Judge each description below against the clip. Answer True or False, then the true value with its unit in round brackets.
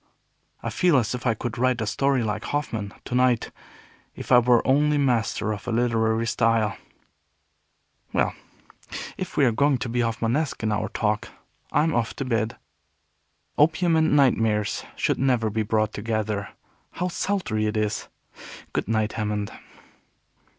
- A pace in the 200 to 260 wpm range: False (150 wpm)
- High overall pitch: False (115 Hz)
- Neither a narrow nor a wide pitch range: True (3.3 semitones)